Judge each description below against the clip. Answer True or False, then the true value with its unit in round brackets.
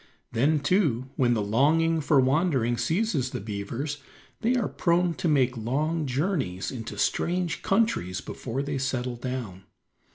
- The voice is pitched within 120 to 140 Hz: True (135 Hz)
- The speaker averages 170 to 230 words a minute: False (140 wpm)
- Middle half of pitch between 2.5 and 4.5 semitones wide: False (5.4 semitones)